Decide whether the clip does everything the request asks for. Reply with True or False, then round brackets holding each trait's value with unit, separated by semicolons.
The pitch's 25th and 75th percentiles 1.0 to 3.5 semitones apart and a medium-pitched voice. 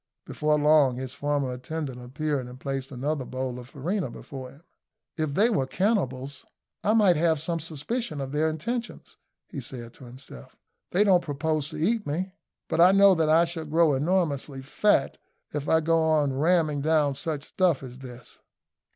False (3.9 semitones; 150 Hz)